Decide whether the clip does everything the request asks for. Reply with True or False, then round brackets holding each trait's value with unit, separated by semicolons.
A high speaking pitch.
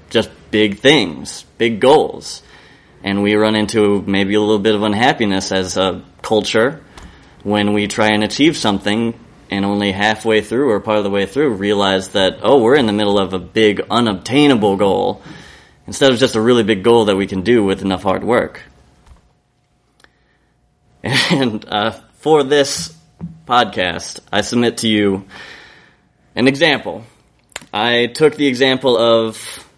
False (105 Hz)